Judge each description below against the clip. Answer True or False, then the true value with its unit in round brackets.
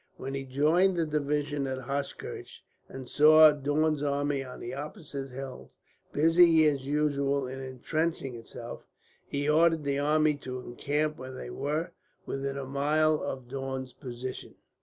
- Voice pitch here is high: False (140 Hz)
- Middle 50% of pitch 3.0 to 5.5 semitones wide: False (2.4 semitones)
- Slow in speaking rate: False (145 wpm)